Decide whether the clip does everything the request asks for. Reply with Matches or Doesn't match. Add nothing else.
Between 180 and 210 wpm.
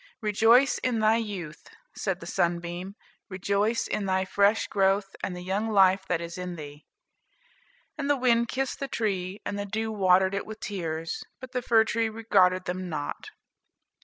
Doesn't match